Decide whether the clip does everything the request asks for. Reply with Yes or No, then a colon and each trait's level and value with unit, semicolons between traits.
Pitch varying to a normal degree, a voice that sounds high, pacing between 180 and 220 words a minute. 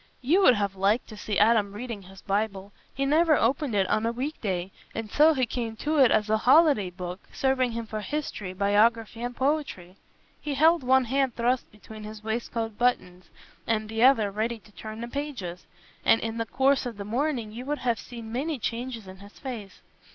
Yes: average, 4.0 semitones; high, 230 Hz; average, 200 wpm